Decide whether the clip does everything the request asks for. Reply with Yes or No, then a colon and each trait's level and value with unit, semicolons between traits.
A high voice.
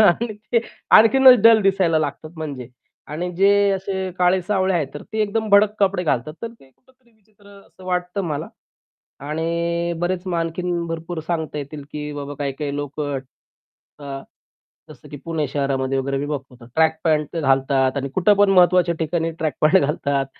No: medium, 165 Hz